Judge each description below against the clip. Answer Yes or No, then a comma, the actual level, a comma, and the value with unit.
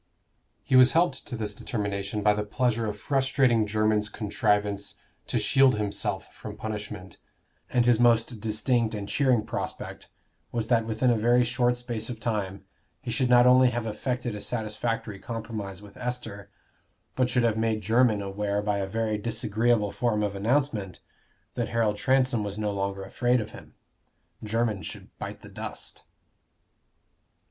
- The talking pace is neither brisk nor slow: Yes, average, 155 wpm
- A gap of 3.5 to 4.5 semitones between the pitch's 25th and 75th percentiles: No, average, 2.8 semitones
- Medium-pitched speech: No, low, 110 Hz